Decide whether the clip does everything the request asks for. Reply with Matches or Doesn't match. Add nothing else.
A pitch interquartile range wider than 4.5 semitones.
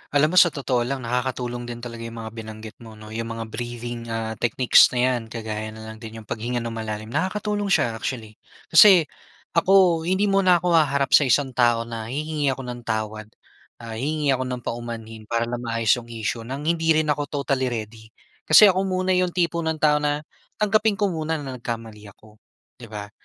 Matches